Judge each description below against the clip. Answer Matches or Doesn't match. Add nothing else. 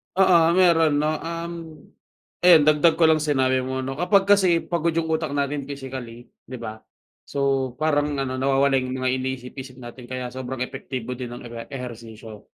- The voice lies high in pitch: Doesn't match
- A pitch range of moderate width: Matches